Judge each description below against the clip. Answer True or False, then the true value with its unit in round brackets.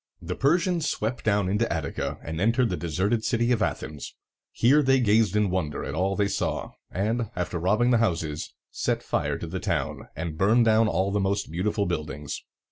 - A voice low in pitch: True (100 Hz)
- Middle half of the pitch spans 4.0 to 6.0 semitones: True (4.9 semitones)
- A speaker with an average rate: True (190 wpm)